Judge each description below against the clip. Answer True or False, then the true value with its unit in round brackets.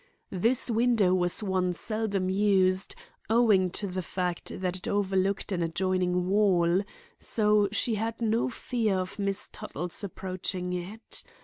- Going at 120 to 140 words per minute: True (135 wpm)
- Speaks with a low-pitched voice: False (190 Hz)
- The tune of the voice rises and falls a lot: False (2.7 semitones)